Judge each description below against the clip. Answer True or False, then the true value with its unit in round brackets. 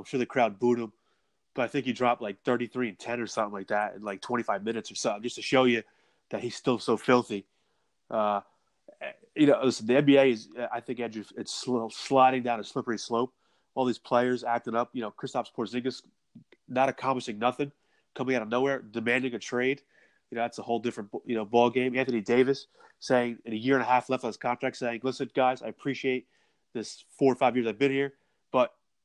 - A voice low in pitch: True (125 Hz)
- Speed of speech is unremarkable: False (215 wpm)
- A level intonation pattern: True (1.9 semitones)